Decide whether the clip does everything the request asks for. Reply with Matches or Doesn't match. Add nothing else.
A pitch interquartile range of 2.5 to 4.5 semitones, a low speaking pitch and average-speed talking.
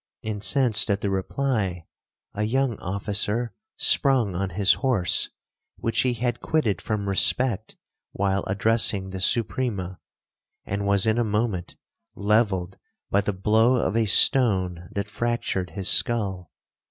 Doesn't match